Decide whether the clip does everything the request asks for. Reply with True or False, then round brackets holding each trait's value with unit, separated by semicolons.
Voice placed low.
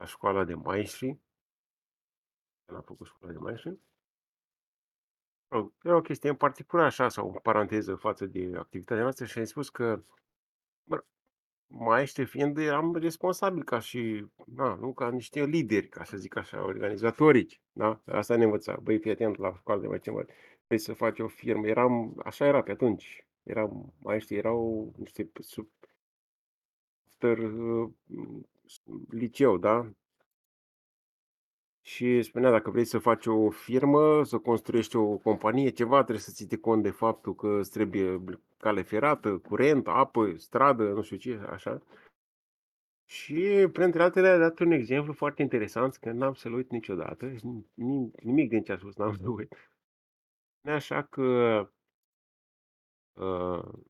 True (115 Hz)